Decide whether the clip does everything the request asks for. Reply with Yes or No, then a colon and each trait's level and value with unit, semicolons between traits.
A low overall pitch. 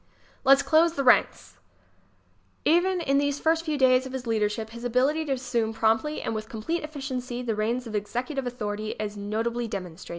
No: very high, 250 Hz